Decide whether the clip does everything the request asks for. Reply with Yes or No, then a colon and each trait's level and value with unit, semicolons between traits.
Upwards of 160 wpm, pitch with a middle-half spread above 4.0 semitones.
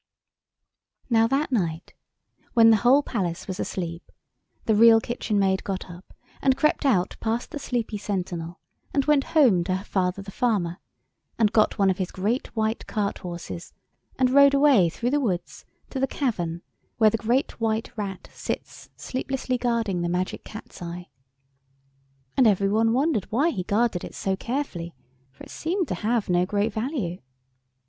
Yes: average, 170 wpm; average, 5.2 semitones